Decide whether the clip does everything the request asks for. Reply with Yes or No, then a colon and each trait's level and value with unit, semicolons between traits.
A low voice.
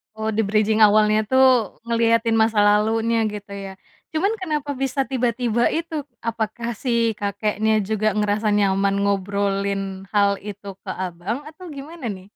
No: high, 215 Hz